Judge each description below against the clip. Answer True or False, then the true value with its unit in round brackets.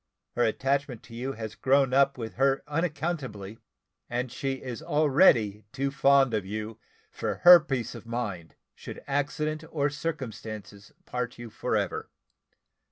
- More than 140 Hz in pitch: False (130 Hz)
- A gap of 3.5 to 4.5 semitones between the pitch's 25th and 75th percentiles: True (4.0 semitones)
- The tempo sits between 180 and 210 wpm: False (145 wpm)